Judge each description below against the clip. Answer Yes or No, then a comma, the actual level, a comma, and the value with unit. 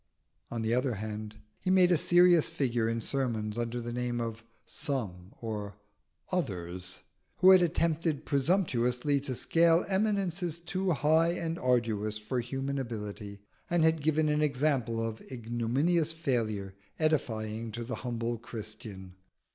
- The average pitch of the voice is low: Yes, low, 125 Hz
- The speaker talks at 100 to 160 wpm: Yes, average, 140 wpm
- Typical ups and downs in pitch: No, wide, 6.2 semitones